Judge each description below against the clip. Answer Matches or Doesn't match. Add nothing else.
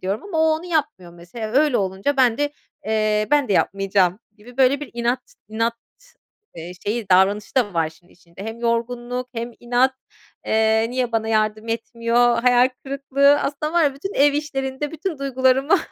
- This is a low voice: Doesn't match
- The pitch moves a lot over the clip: Doesn't match